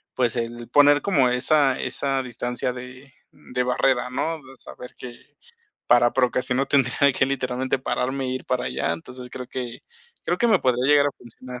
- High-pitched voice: No, low, 130 Hz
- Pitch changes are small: Yes, narrow, 1.7 semitones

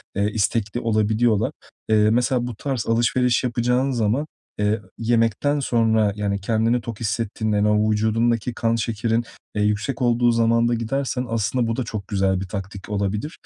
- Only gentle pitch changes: Yes, narrow, 2.2 semitones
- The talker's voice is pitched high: No, low, 115 Hz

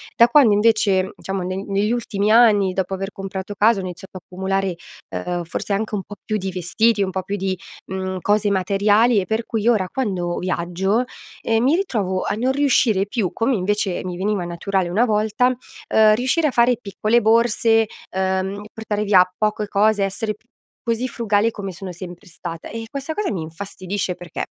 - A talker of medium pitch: No, high, 205 Hz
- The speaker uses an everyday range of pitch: Yes, average, 3.0 semitones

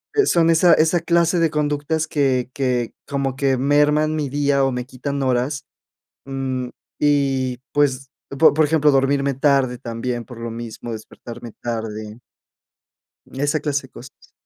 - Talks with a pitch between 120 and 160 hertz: Yes, low, 135 Hz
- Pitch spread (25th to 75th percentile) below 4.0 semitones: Yes, average, 2.9 semitones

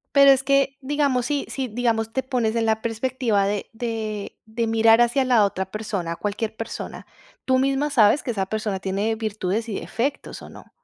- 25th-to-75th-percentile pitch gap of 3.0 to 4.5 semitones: Yes, average, 3.5 semitones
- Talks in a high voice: Yes, high, 225 Hz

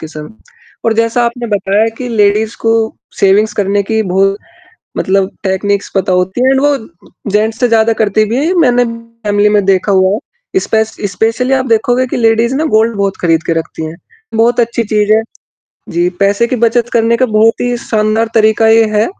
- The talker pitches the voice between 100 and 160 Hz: No, high, 220 Hz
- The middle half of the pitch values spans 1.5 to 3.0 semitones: Yes, narrow, 2.6 semitones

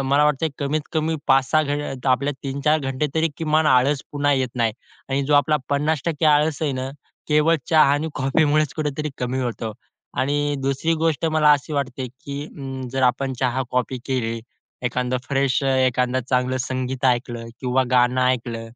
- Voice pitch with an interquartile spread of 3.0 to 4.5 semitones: No, narrow, 2.6 semitones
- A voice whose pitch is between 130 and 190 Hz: Yes, low, 135 Hz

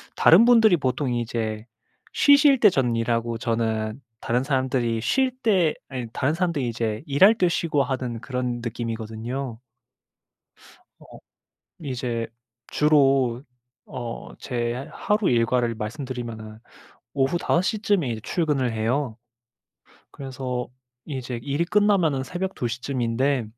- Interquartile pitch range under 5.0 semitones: Yes, average, 4.4 semitones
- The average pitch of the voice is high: No, low, 130 Hz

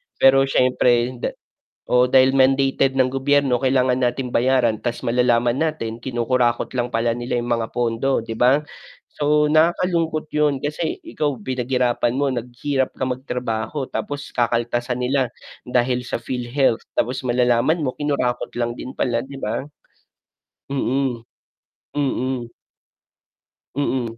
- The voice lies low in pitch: Yes, low, 125 Hz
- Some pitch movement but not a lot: No, narrow, 2.2 semitones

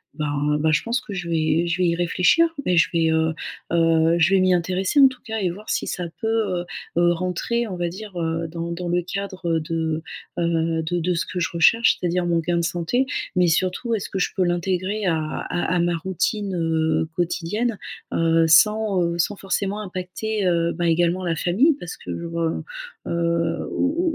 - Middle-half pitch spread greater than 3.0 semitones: No, average, 2.7 semitones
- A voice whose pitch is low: No, medium, 175 Hz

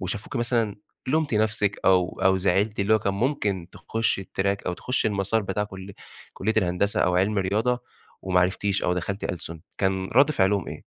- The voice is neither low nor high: No, low, 100 Hz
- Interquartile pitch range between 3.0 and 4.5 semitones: No, narrow, 2.5 semitones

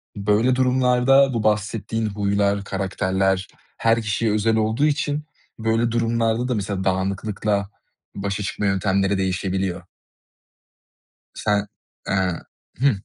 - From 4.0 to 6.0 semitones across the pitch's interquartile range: No, average, 2.9 semitones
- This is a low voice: Yes, low, 105 Hz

